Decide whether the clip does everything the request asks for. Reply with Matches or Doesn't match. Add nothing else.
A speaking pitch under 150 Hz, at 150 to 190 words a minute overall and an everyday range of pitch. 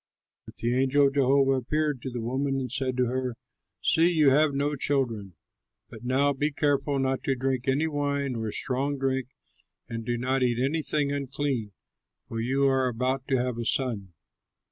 Doesn't match